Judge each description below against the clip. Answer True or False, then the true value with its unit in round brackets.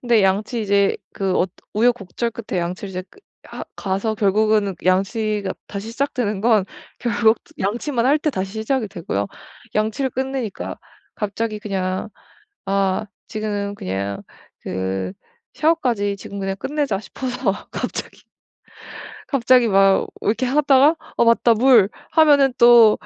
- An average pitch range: True (3.9 semitones)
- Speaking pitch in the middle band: False (215 Hz)